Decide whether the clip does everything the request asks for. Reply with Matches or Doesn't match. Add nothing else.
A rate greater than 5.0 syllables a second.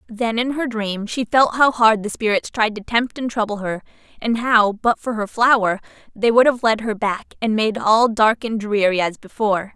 Doesn't match